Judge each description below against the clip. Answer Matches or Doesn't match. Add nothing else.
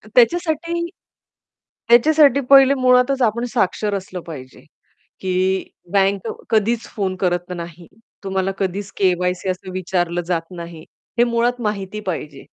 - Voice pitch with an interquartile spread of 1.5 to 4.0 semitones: Doesn't match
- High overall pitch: Matches